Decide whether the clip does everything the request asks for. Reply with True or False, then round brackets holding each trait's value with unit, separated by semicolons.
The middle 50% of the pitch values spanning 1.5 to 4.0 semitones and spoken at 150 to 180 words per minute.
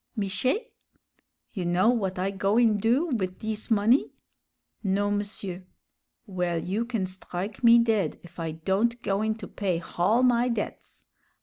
False (3.7 semitones; 140 wpm)